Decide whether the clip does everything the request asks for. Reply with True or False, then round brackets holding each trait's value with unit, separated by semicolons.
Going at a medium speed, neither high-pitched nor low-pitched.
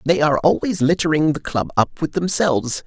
True (190 wpm; 155 Hz)